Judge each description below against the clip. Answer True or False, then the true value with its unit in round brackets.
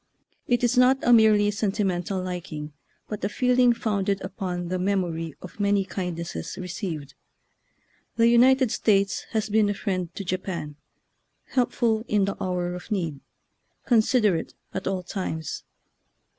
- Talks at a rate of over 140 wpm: False (135 wpm)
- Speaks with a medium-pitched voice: False (195 Hz)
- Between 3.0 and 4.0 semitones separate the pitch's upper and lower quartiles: True (3.5 semitones)